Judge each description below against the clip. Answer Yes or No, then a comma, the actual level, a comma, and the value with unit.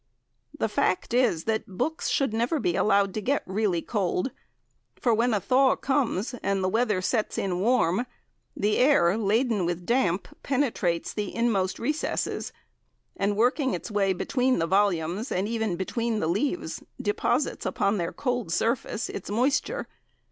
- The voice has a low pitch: No, high, 215 Hz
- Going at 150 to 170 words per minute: Yes, average, 155 wpm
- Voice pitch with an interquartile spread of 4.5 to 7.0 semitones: Yes, average, 4.8 semitones